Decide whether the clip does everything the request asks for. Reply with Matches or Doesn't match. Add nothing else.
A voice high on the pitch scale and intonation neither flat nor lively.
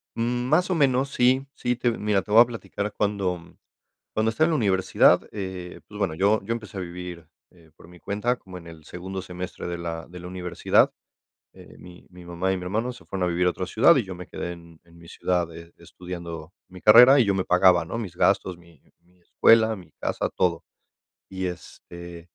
Doesn't match